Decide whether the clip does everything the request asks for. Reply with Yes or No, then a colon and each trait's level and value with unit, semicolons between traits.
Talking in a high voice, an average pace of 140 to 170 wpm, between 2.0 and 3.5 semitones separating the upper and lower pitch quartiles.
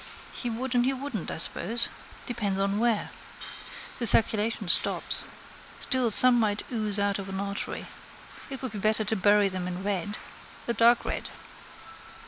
Yes: high, 215 Hz; average, 160 wpm; average, 3.1 semitones